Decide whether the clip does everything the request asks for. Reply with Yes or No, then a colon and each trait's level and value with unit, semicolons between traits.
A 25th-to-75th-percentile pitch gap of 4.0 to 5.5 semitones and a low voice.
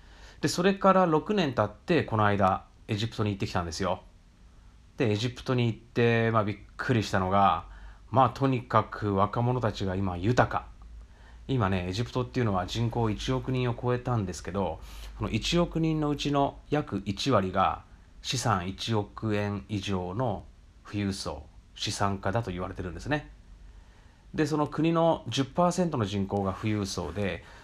Yes: average, 5.1 semitones; low, 105 Hz